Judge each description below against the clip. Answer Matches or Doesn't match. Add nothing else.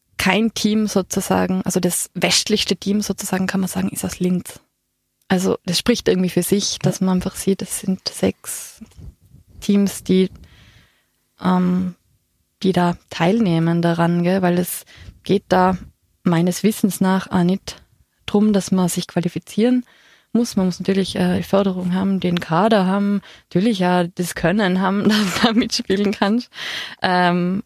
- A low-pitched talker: Doesn't match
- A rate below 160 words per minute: Matches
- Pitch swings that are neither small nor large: Doesn't match